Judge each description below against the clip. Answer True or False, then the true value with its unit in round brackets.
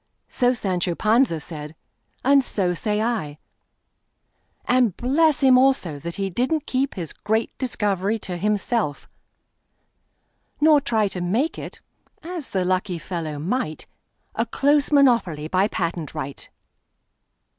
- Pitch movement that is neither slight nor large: False (6.6 semitones)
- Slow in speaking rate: True (115 wpm)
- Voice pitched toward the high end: True (210 Hz)